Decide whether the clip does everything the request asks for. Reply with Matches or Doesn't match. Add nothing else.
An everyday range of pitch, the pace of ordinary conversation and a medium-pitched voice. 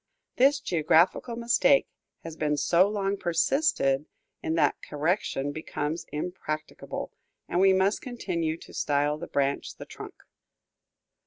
Doesn't match